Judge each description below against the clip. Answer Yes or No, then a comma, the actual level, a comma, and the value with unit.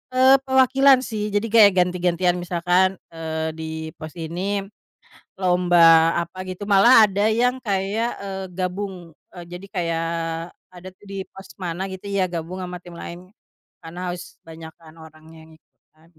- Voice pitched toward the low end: No, medium, 180 Hz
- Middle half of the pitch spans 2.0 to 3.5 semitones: Yes, average, 3.0 semitones